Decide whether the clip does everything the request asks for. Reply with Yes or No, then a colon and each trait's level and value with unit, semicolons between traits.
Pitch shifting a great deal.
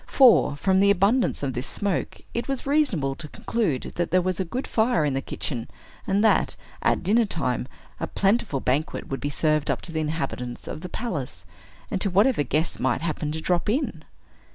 Yes: wide, 6.2 semitones